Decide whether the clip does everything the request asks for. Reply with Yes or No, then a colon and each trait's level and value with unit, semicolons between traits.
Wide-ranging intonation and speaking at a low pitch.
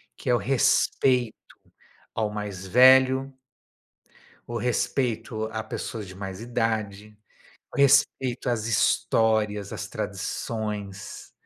No: average, 3.1 semitones; low, 110 Hz